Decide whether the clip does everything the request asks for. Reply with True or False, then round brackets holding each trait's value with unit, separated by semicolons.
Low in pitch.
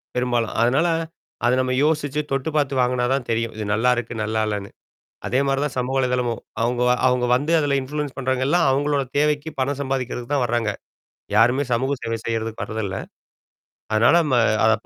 True (125 Hz)